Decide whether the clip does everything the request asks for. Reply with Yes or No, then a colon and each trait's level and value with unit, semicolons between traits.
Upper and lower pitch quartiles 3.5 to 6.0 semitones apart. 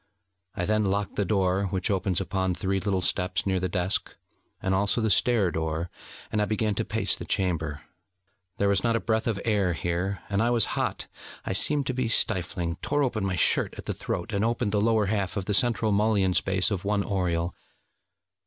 No: average, 2.7 semitones